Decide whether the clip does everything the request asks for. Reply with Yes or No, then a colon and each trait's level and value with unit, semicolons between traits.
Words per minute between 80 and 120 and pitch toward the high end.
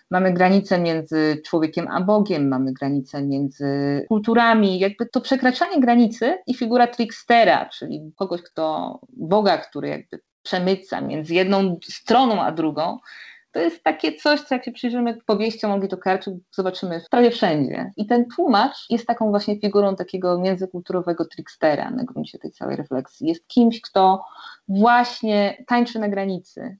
No: average, 145 wpm; high, 195 Hz